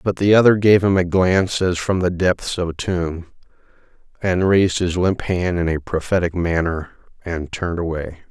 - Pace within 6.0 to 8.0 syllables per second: No, 5.1 syllables/s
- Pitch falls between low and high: No, very low, 90 Hz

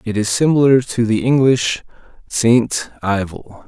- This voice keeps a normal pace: No, slow, 130 wpm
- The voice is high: No, low, 115 Hz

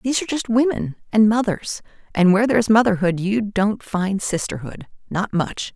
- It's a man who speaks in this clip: No, female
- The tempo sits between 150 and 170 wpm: Yes, average, 155 wpm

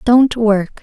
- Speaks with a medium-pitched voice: No, high, 225 Hz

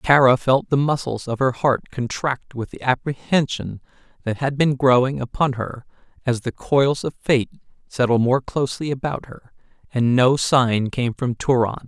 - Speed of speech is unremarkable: Yes, average, 165 wpm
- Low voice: Yes, low, 130 Hz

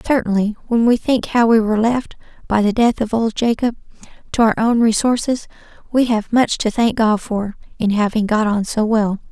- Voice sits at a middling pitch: No, high, 225 Hz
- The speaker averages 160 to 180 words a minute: No, average, 200 wpm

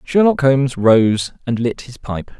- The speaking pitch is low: Yes, low, 130 Hz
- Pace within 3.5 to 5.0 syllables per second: Yes, 4.2 syllables/s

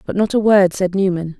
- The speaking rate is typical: No, fast, 260 wpm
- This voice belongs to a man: No, female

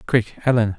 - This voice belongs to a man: Yes, male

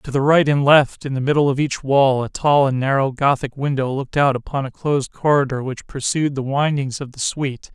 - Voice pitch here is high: No, low, 135 Hz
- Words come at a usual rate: No, fast, 230 wpm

